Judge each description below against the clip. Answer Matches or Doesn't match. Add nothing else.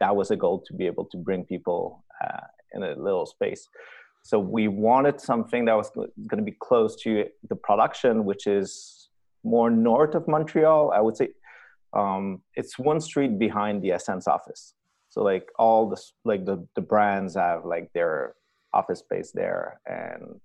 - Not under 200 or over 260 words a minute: Doesn't match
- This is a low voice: Matches